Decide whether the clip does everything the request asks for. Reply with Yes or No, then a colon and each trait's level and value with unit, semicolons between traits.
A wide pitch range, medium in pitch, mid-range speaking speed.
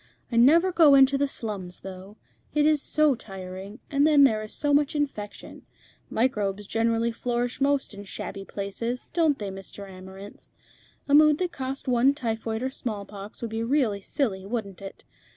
No: wide, 5.8 semitones; high, 230 Hz; average, 170 wpm